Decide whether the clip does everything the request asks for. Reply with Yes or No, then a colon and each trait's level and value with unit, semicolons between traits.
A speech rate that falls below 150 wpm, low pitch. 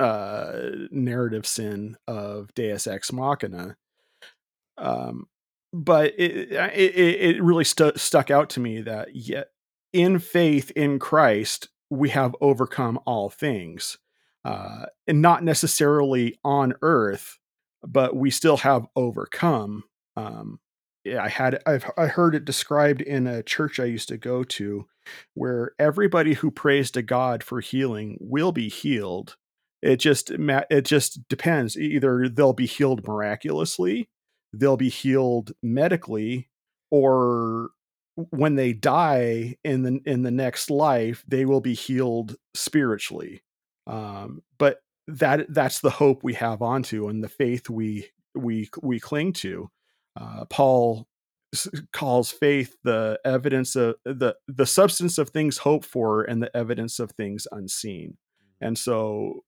Yes: slow, 135 wpm; low, 130 Hz